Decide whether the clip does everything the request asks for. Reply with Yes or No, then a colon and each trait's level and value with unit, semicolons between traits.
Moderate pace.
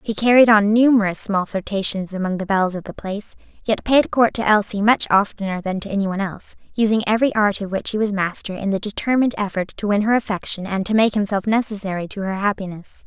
No: fast, 220 wpm